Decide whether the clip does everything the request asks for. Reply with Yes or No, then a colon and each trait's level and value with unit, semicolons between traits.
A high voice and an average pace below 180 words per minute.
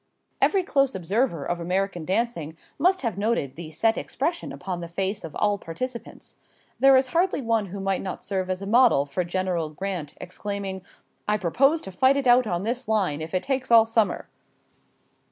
No: high, 200 Hz; average, 185 wpm